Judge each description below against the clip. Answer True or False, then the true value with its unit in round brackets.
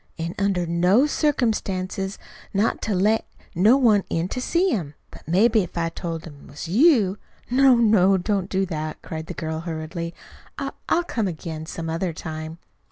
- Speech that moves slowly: False (180 wpm)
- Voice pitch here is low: False (185 Hz)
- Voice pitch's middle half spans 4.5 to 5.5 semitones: True (4.8 semitones)